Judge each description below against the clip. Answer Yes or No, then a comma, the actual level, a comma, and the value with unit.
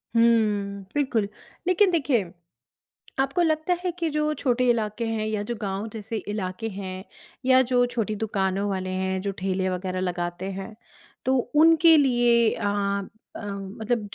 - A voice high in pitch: Yes, high, 220 Hz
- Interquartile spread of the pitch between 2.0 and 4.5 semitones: No, average, 5.2 semitones